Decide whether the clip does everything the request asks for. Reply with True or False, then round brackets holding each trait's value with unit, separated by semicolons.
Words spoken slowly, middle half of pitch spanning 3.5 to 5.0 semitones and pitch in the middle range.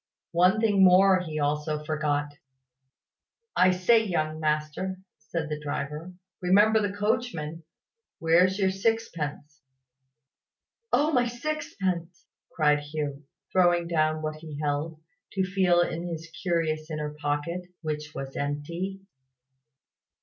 True (115 wpm; 3.9 semitones; 165 Hz)